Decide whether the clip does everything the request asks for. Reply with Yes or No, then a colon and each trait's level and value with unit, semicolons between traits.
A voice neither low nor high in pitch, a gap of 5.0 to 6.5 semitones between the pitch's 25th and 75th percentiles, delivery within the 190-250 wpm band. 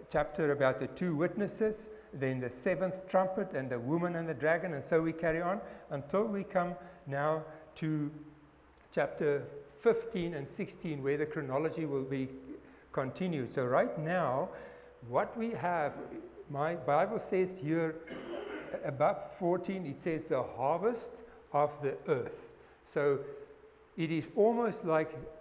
No: medium, 170 Hz; wide, 5.4 semitones; average, 140 wpm